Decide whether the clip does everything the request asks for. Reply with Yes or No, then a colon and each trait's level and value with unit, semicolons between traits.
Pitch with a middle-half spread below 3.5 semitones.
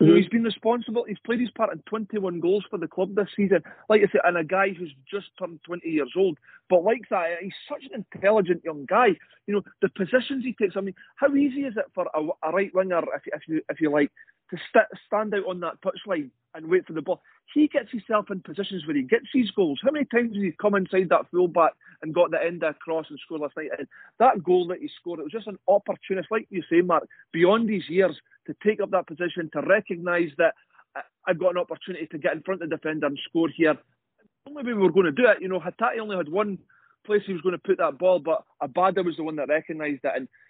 No: average, 3.8 semitones